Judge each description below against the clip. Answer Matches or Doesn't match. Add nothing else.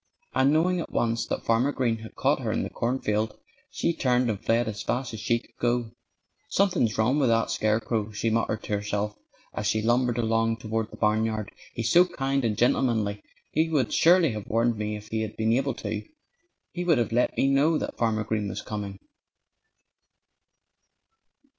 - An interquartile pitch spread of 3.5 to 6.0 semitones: Doesn't match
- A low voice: Matches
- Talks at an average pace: Matches